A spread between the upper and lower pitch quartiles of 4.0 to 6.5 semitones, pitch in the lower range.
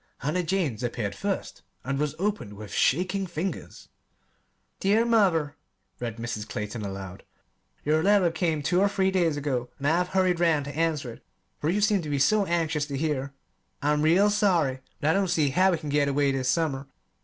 No: average, 5.2 semitones; medium, 155 Hz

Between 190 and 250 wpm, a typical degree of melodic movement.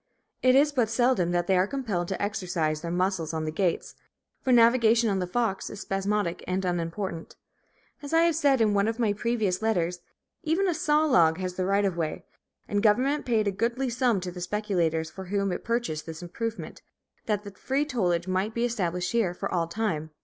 Yes: average, 200 wpm; average, 4.8 semitones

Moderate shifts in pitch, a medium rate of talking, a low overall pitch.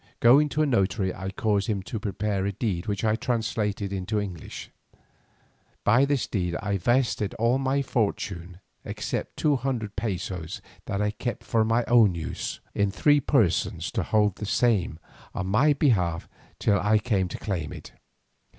Yes: average, 3.9 semitones; average, 165 wpm; low, 105 Hz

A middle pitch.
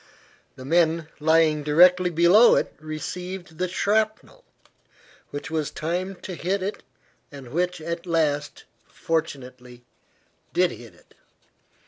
Yes: medium, 165 Hz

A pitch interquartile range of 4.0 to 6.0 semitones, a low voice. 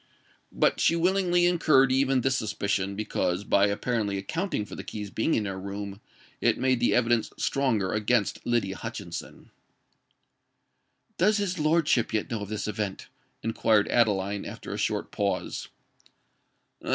Yes: average, 4.9 semitones; low, 110 Hz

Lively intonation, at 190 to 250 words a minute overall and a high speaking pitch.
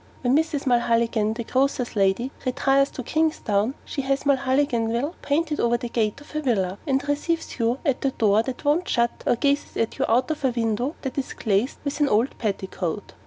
No: average, 3.7 semitones; average, 195 wpm; very high, 255 Hz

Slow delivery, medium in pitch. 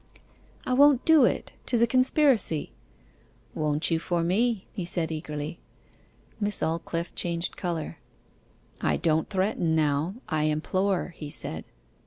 Yes: slow, 130 wpm; medium, 170 Hz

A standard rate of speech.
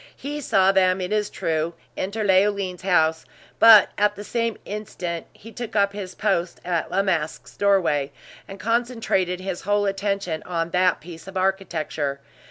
Yes: average, 160 wpm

